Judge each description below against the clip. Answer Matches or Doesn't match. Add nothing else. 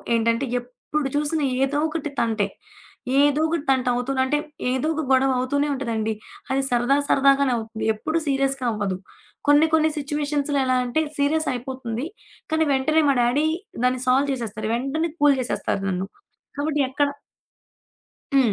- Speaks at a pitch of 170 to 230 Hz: Doesn't match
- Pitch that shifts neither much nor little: Matches